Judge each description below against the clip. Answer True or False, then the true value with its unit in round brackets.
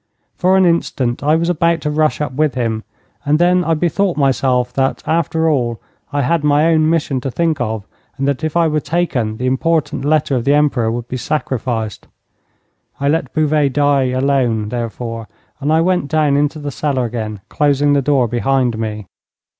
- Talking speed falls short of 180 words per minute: False (185 wpm)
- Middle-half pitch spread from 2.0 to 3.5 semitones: False (4.1 semitones)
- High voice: False (140 Hz)